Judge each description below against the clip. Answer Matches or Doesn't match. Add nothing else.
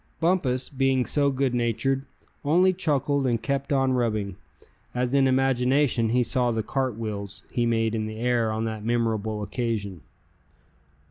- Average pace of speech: Matches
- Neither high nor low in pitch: Doesn't match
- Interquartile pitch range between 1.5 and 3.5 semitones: Matches